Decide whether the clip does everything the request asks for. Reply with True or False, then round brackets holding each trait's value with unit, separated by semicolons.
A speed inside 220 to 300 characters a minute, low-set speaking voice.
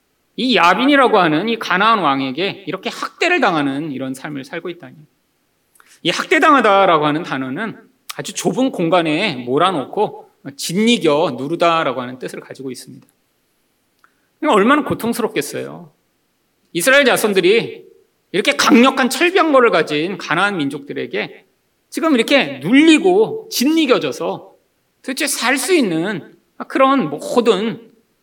False (295 characters per minute; 230 Hz)